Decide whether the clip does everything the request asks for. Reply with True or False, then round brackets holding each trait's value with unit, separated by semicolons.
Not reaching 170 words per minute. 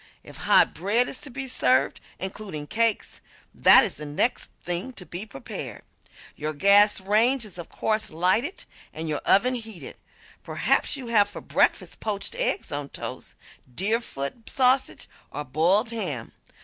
True (150 wpm)